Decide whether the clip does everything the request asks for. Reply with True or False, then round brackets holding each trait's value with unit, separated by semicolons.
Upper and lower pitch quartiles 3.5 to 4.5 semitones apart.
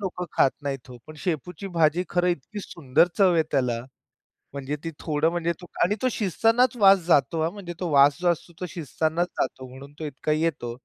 True (3.9 semitones)